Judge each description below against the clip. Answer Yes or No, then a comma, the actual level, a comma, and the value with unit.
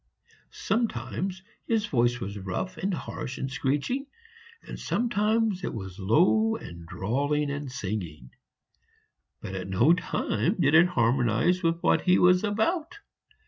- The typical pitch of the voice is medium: Yes, medium, 150 Hz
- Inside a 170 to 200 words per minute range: No, slow, 135 wpm